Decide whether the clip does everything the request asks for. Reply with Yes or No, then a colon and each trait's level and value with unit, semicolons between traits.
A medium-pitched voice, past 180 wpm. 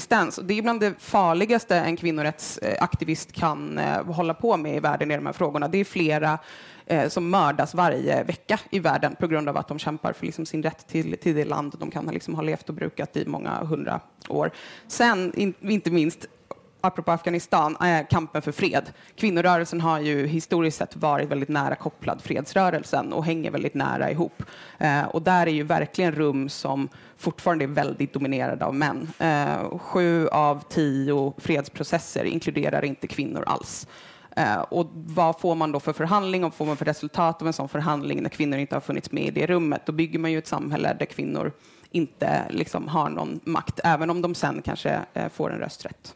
Yes: medium, 160 Hz; average, 190 wpm